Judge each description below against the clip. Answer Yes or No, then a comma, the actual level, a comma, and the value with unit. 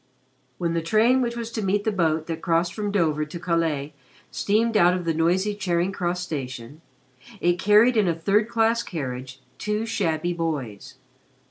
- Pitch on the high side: No, medium, 175 Hz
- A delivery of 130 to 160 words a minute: No, average, 170 wpm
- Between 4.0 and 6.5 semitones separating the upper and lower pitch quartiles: Yes, average, 4.5 semitones